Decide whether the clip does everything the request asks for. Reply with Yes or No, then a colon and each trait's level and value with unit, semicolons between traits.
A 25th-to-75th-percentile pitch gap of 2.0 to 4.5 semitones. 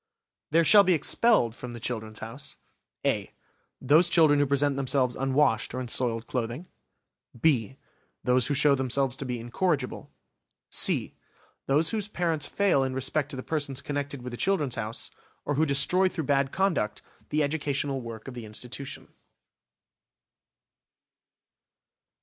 Yes: average, 3.6 semitones